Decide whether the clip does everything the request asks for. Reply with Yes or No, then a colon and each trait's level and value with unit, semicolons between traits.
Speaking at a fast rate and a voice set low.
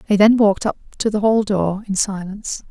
No: fast, 220 wpm; high, 205 Hz